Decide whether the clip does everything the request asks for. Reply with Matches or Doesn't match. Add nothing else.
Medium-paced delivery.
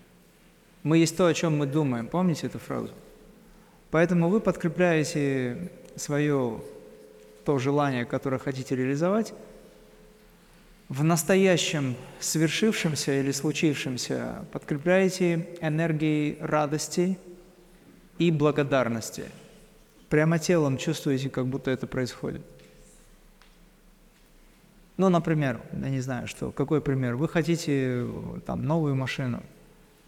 Doesn't match